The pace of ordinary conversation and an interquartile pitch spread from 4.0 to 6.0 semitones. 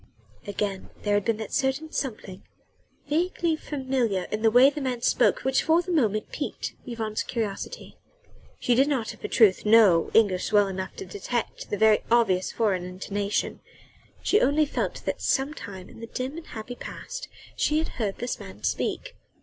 Yes: average, 175 wpm; average, 5.0 semitones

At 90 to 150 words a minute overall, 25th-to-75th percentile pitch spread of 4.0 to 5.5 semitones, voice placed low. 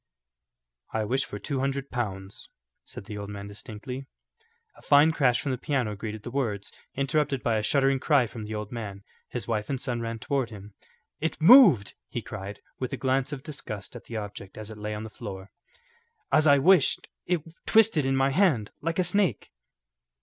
No: average, 195 wpm; average, 4.9 semitones; low, 125 Hz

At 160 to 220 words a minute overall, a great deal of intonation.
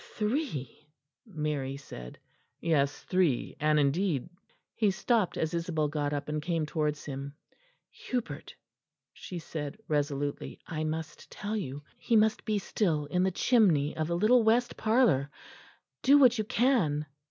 No: average, 145 wpm; wide, 6.5 semitones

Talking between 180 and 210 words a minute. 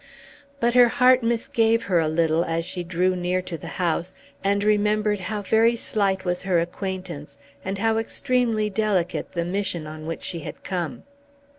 No: average, 170 wpm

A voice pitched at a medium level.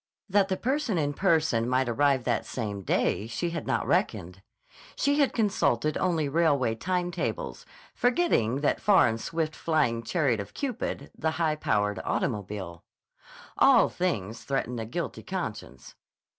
Yes: medium, 145 Hz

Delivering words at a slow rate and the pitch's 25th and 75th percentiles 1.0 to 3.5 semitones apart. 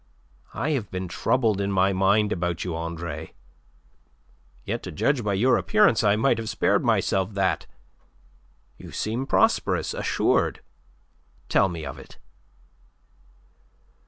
No: slow, 125 wpm; average, 4.3 semitones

